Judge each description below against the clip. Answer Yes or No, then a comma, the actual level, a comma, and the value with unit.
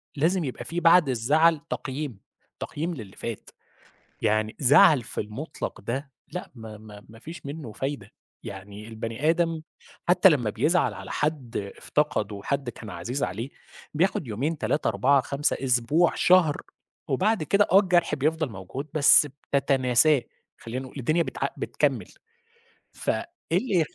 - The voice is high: No, medium, 140 Hz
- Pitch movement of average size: No, wide, 6.1 semitones